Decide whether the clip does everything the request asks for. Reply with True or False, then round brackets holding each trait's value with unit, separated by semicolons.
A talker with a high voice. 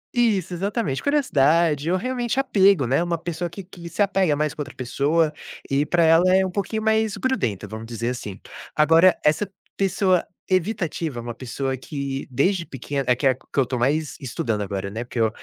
False (160 Hz)